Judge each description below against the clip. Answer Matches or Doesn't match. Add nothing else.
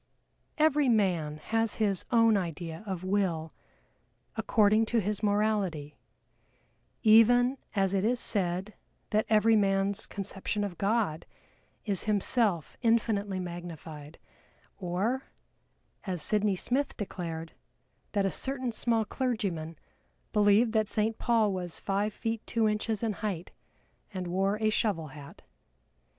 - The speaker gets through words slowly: Matches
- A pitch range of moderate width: Matches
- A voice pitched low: Doesn't match